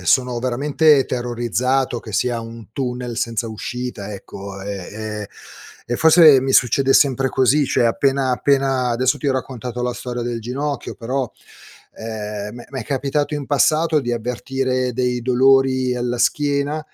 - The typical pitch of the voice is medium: No, low, 125 Hz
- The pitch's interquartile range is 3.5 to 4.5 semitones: No, narrow, 2.5 semitones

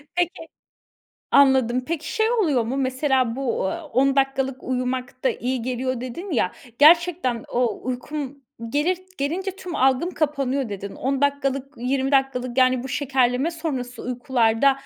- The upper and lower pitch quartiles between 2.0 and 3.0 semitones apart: Yes, narrow, 2.5 semitones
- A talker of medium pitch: No, very high, 265 Hz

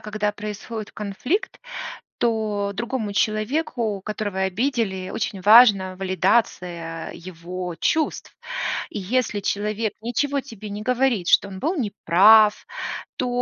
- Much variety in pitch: No, average, 3.5 semitones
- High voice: Yes, high, 210 Hz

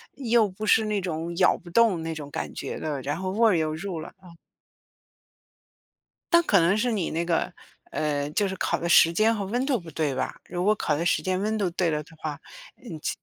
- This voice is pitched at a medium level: Yes, medium, 180 Hz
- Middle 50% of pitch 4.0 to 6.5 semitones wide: Yes, average, 4.9 semitones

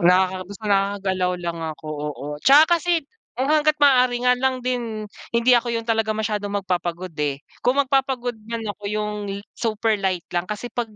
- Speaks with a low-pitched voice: No, high, 215 Hz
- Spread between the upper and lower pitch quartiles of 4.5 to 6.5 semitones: Yes, average, 5.0 semitones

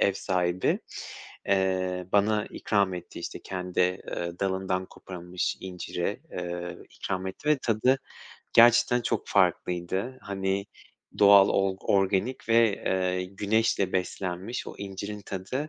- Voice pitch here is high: No, very low, 95 Hz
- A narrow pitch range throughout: Yes, narrow, 2.2 semitones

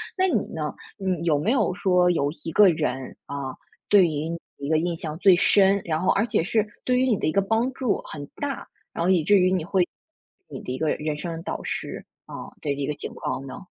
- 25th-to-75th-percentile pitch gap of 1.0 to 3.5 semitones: No, average, 4.5 semitones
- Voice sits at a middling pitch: Yes, medium, 175 Hz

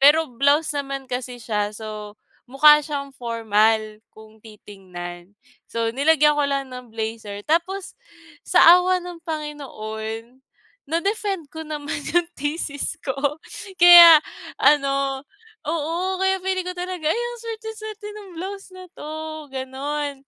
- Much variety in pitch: Yes, wide, 6.7 semitones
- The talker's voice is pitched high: Yes, very high, 285 Hz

